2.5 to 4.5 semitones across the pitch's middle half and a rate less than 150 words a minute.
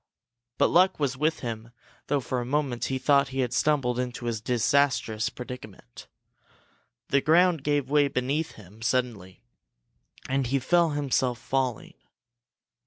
Yes: average, 3.1 semitones; average, 140 wpm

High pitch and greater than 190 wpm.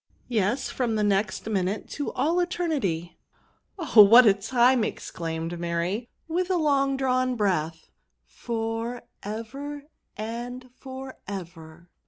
No: high, 225 Hz; average, 140 wpm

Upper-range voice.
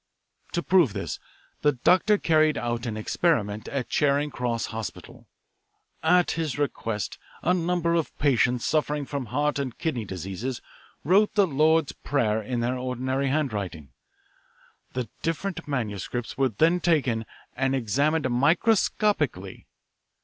No: low, 135 Hz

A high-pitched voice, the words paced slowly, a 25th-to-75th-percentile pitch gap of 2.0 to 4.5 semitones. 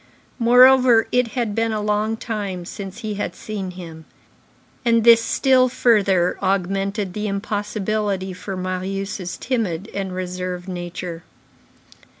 Yes: high, 200 Hz; slow, 125 wpm; average, 3.4 semitones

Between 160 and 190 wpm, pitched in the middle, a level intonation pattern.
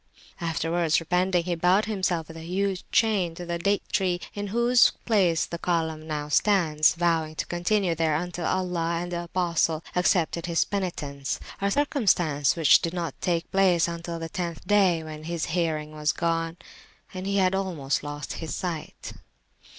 Yes: average, 165 wpm; medium, 170 Hz; narrow, 2.3 semitones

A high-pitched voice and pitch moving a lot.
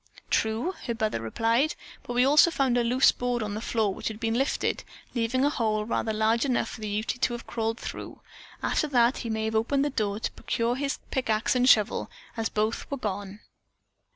No: high, 230 Hz; narrow, 2.6 semitones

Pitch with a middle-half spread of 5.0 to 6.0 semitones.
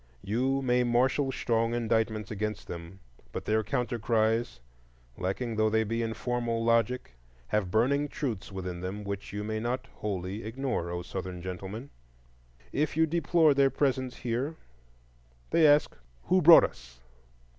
No: average, 4.2 semitones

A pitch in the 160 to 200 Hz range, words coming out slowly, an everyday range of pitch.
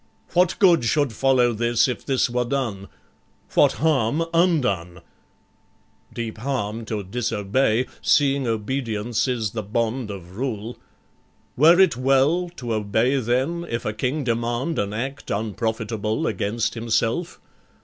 No: low, 120 Hz; slow, 130 wpm; average, 3.9 semitones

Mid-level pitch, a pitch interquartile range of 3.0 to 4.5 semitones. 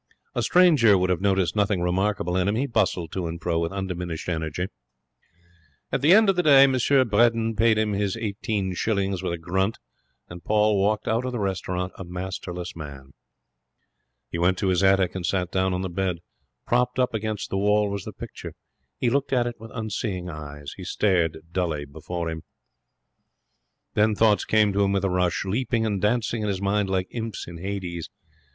No: very low, 95 Hz; average, 3.5 semitones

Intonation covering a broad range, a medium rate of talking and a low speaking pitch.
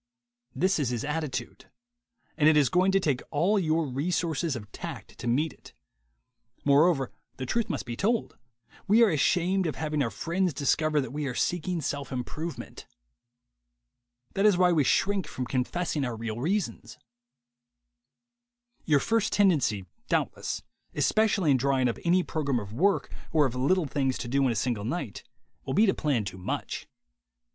No: wide, 5.7 semitones; average, 170 wpm; medium, 150 Hz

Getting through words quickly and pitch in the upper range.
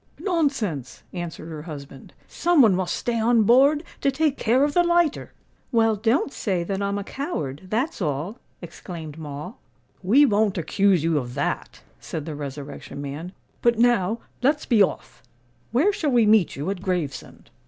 No: average, 165 wpm; high, 200 Hz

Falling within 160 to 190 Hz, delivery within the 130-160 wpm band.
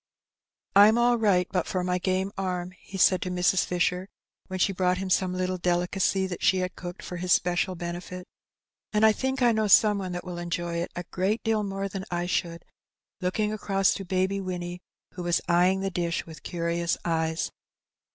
No: medium, 185 Hz; average, 200 wpm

